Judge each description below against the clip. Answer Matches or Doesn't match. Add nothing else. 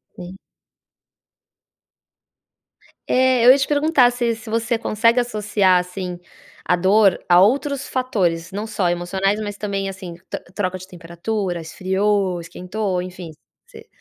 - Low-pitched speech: Doesn't match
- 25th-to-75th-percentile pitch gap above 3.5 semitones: Matches